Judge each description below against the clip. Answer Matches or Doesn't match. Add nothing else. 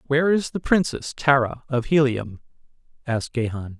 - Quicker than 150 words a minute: Doesn't match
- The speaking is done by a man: Matches